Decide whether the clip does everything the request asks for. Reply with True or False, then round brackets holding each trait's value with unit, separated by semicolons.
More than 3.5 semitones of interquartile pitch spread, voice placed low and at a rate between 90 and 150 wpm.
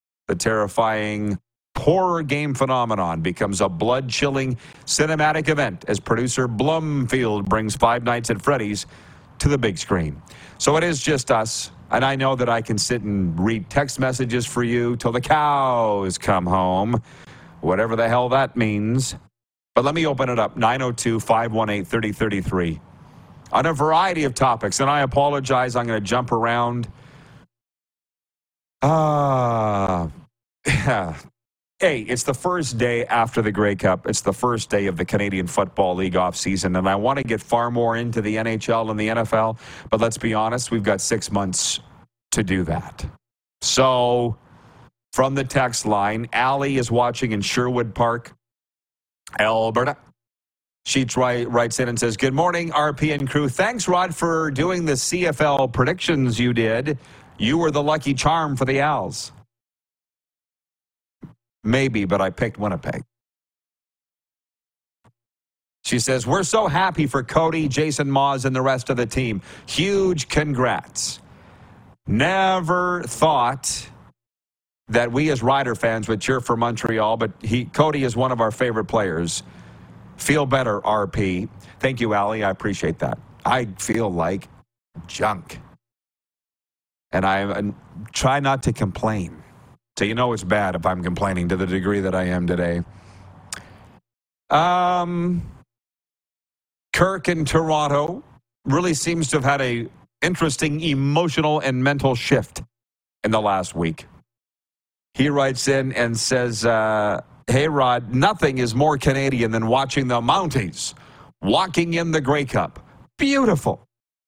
True (4.7 semitones; 120 Hz; 145 wpm)